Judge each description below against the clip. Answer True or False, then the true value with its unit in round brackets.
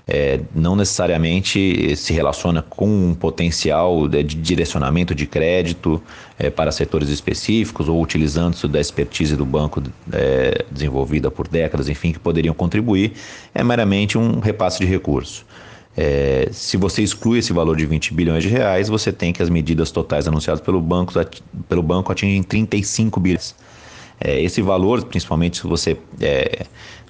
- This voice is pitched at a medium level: False (85 Hz)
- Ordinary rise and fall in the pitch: True (3.8 semitones)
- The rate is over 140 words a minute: True (150 wpm)